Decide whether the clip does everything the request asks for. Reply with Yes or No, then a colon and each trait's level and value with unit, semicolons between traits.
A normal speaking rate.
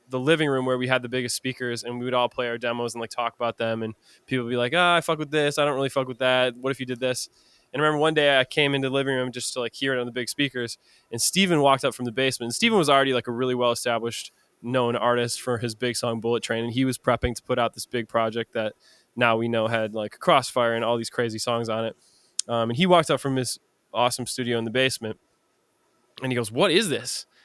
No: fast, 280 wpm